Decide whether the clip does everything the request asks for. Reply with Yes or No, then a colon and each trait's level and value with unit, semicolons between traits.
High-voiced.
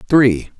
No: low, 120 Hz